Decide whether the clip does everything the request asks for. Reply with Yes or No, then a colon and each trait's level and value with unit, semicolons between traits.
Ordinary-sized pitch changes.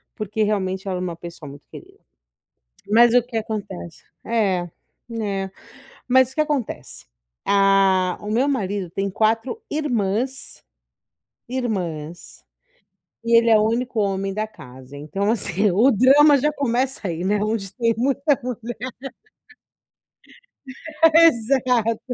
Yes: average, 4.4 semitones